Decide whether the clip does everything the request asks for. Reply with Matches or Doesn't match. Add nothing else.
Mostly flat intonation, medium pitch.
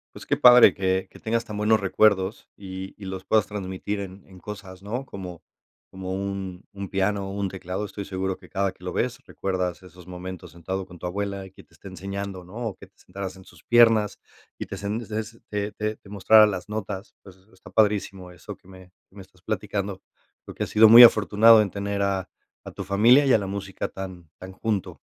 Doesn't match